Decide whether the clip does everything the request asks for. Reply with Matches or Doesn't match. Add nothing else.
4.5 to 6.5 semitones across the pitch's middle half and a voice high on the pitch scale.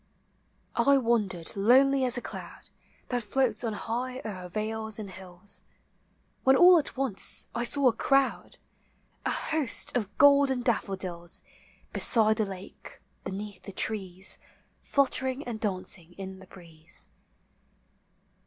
Matches